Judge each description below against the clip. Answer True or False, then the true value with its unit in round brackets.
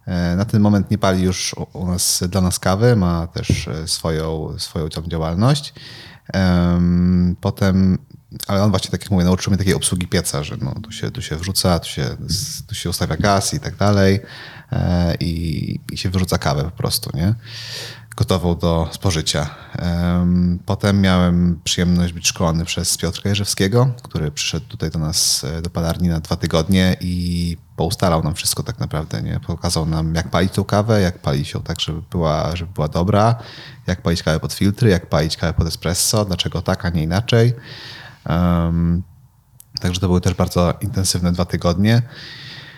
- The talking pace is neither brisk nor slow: False (170 wpm)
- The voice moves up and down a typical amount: True (3.5 semitones)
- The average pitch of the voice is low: True (90 Hz)